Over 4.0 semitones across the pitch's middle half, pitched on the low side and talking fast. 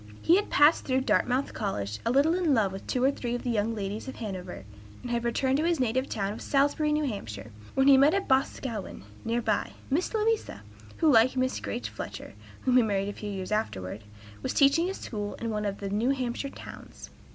No: average, 5.1 semitones; high, 245 Hz; fast, 215 wpm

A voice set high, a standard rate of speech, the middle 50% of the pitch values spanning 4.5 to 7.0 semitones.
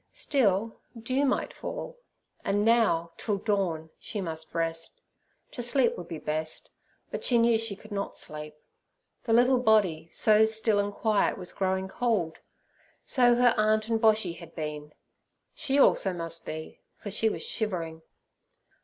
Yes: high, 205 Hz; average, 150 wpm; average, 5.3 semitones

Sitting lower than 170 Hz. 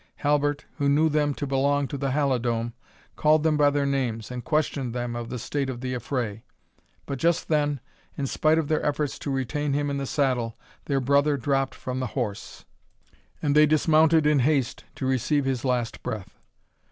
Yes: medium, 140 Hz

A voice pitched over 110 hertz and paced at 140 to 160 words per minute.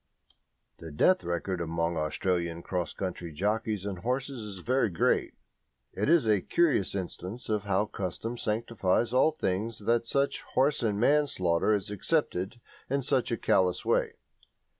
No: low, 105 Hz; average, 150 wpm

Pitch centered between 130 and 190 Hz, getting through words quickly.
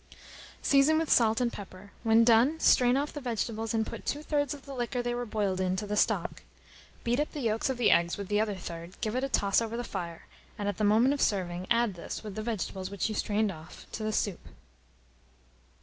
No: high, 220 Hz; fast, 230 wpm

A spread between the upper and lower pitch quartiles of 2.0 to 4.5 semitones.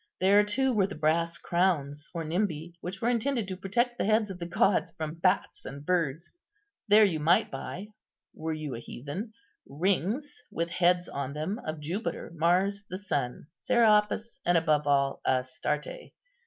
No: average, 5.2 semitones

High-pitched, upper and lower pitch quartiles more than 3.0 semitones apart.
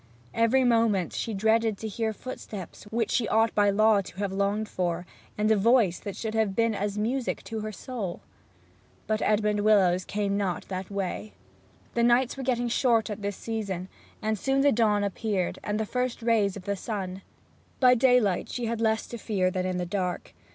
No: high, 215 Hz; average, 2.7 semitones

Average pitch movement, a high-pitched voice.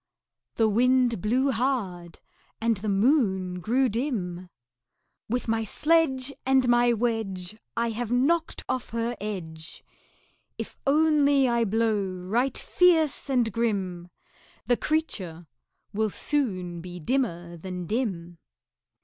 No: wide, 5.8 semitones; high, 225 Hz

